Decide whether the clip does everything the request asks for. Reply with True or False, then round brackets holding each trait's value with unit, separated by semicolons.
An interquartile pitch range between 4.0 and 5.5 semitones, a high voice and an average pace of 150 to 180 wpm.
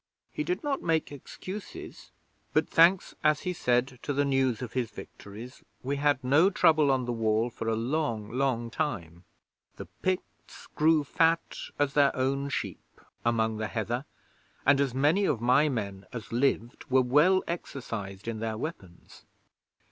False (4.8 semitones; 130 Hz; 160 wpm)